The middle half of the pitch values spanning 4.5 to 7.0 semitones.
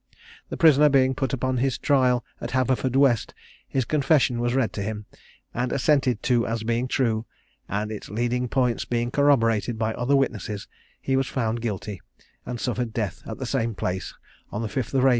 No: average, 2.8 semitones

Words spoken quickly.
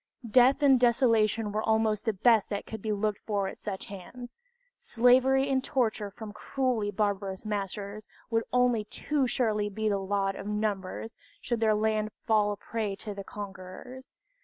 No: average, 165 wpm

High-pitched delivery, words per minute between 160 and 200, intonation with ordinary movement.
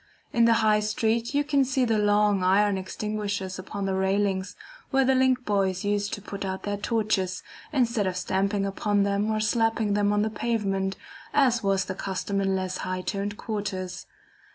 No: high, 205 Hz; average, 180 wpm; narrow, 2.3 semitones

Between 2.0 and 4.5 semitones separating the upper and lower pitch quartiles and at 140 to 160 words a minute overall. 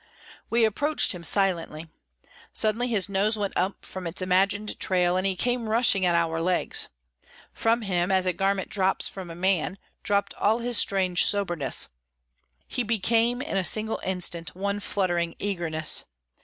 Yes: average, 3.2 semitones; average, 155 wpm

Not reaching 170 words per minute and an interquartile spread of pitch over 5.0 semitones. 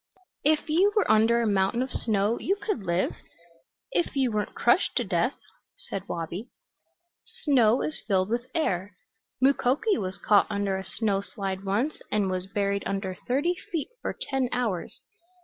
Yes: average, 160 wpm; wide, 5.4 semitones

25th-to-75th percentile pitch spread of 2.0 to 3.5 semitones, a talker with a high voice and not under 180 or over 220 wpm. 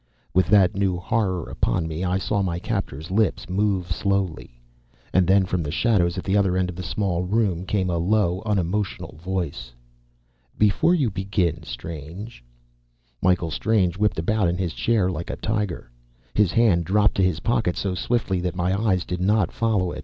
No: average, 3.1 semitones; very low, 95 Hz; average, 185 wpm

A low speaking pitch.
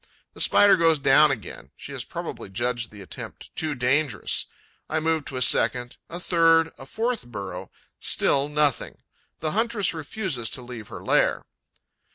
No: medium, 145 Hz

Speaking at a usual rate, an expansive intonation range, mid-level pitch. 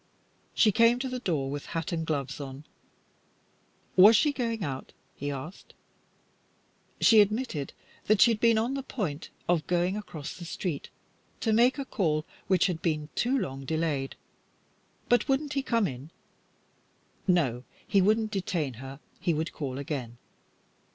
Yes: average, 160 wpm; wide, 7.7 semitones; medium, 175 Hz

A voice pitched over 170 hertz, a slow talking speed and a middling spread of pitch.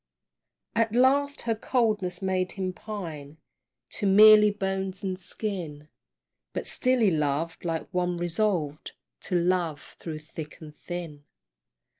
Yes: medium, 185 Hz; slow, 125 wpm; average, 4.6 semitones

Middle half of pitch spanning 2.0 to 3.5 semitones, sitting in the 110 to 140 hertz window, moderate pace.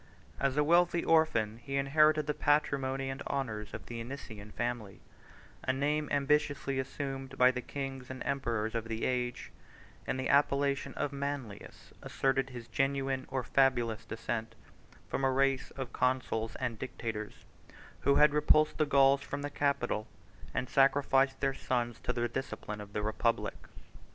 Yes: average, 2.9 semitones; low, 135 Hz; average, 155 wpm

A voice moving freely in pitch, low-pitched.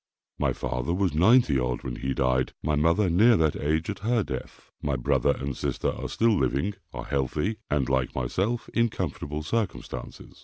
Yes: wide, 7.6 semitones; very low, 75 Hz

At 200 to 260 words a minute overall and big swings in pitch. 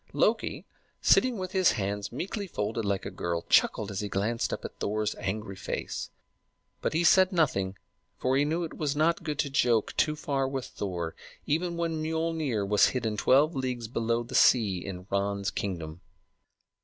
No: average, 175 wpm; wide, 7.7 semitones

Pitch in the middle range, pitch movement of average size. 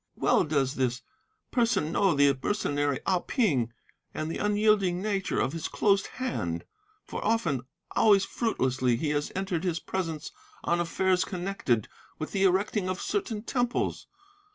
No: medium, 180 Hz; wide, 6.0 semitones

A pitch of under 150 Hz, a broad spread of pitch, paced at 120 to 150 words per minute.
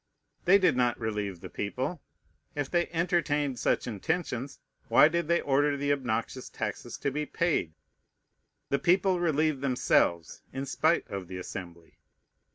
Yes: medium, 140 Hz; wide, 6.1 semitones; average, 145 wpm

